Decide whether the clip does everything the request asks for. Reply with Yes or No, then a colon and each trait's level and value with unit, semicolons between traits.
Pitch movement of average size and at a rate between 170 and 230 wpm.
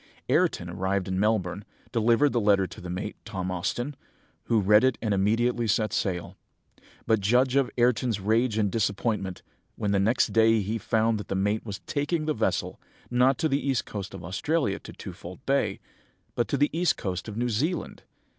Yes: average, 3.8 semitones; average, 185 wpm